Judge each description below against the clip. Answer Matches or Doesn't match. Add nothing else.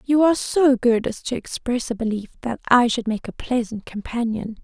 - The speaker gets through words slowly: Doesn't match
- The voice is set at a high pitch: Matches